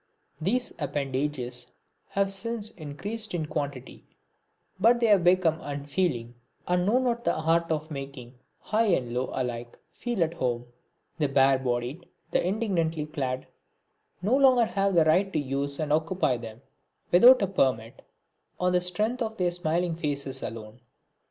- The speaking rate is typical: Yes, average, 150 wpm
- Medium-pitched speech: Yes, medium, 160 Hz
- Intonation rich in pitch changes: Yes, wide, 6.4 semitones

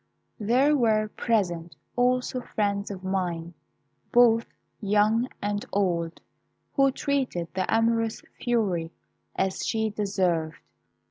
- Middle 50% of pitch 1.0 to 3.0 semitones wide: No, average, 4.0 semitones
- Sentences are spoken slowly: Yes, slow, 105 wpm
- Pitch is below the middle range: No, high, 210 Hz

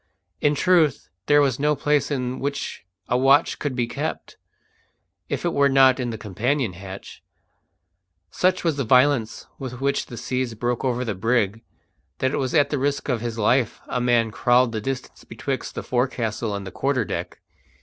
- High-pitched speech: No, low, 125 Hz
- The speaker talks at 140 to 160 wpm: No, average, 180 wpm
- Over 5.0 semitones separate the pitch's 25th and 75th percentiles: No, average, 3.3 semitones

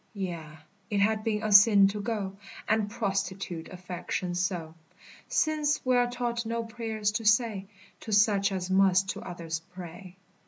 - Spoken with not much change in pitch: No, average, 3.3 semitones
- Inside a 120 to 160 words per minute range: Yes, average, 155 wpm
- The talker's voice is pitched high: Yes, high, 200 Hz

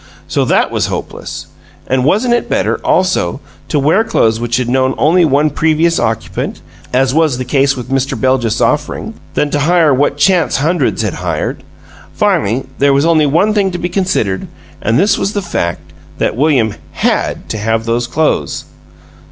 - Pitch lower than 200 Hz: Yes, medium, 140 Hz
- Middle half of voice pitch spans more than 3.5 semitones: Yes, average, 5.2 semitones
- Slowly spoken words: No, average, 175 wpm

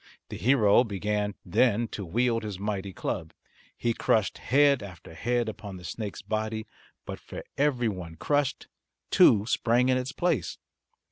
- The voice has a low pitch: Yes, low, 110 Hz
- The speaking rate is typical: Yes, average, 150 wpm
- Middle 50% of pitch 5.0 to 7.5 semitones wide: No, average, 3.5 semitones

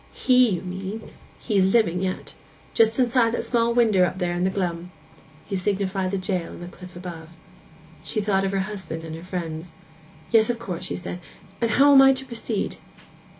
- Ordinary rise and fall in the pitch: Yes, average, 4.1 semitones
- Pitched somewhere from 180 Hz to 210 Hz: Yes, high, 190 Hz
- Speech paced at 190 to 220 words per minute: Yes, average, 195 wpm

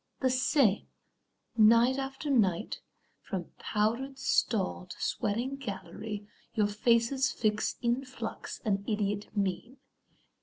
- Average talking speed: No, slow, 110 wpm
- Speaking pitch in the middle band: No, high, 225 Hz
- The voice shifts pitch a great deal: No, average, 4.2 semitones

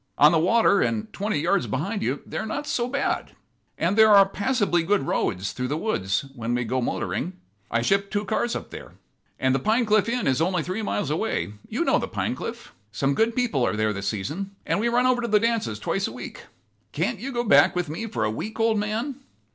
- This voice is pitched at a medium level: No, high, 200 Hz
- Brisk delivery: Yes, fast, 225 wpm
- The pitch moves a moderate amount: No, wide, 8.7 semitones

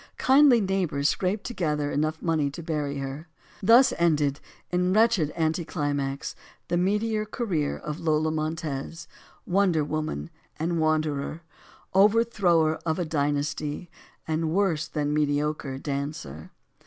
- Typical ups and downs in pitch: Yes, average, 3.6 semitones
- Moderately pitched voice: Yes, medium, 155 Hz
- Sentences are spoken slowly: Yes, slow, 120 wpm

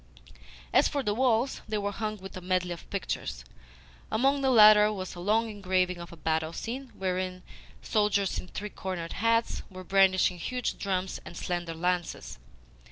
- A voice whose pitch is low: No, high, 190 Hz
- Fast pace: No, average, 165 wpm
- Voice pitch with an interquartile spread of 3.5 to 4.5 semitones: No, average, 3.1 semitones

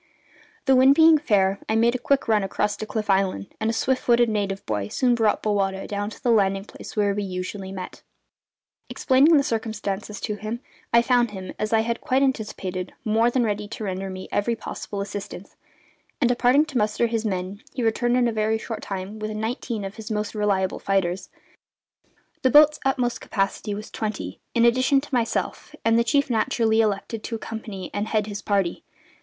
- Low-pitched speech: No, high, 215 Hz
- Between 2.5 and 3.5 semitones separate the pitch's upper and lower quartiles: Yes, average, 3.2 semitones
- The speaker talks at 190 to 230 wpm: Yes, average, 195 wpm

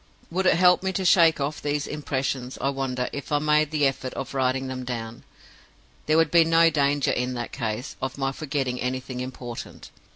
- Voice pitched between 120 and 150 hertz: Yes, low, 135 Hz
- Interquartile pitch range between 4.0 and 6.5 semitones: No, average, 3.1 semitones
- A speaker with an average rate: Yes, average, 195 wpm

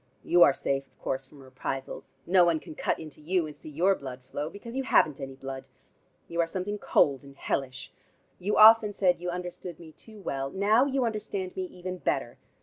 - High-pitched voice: No, medium, 170 Hz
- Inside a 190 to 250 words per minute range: Yes, fast, 205 wpm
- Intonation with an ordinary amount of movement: No, wide, 5.8 semitones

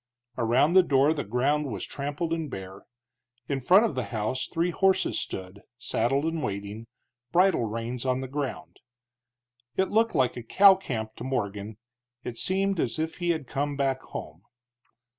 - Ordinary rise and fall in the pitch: No, wide, 6.1 semitones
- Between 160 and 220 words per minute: Yes, average, 165 wpm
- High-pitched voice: No, low, 135 Hz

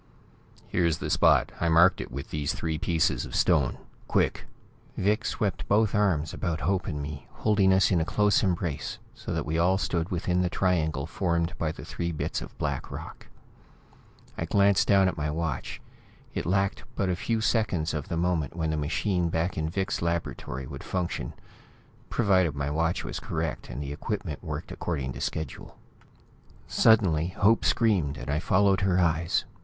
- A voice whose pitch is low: Yes, very low, 85 Hz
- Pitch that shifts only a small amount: No, average, 3.6 semitones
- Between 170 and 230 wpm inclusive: Yes, average, 175 wpm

